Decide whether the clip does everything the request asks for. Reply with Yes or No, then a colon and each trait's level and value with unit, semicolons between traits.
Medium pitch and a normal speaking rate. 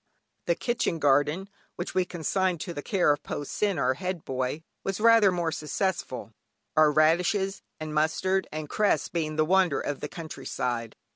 Yes: medium, 160 Hz; average, 170 wpm